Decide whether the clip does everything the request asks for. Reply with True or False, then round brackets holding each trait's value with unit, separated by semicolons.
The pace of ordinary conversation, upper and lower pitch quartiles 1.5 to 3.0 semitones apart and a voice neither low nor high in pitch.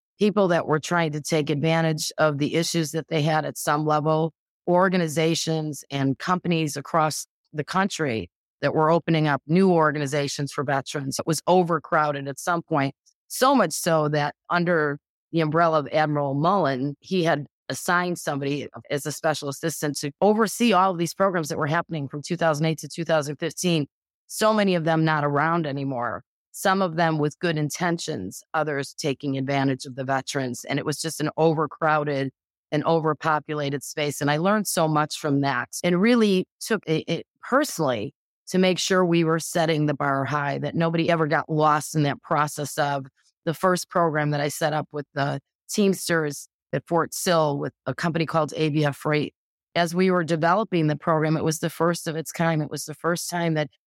True (180 wpm; 2.5 semitones; 155 Hz)